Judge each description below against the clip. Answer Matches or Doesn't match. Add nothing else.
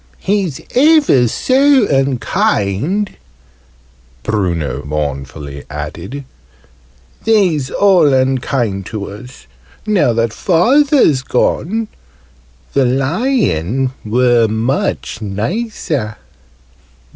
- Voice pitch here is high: Doesn't match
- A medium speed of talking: Doesn't match